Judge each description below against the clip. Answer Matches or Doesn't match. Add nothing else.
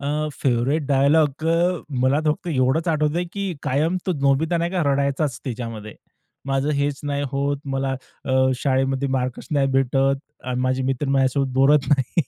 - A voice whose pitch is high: Doesn't match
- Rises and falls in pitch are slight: Matches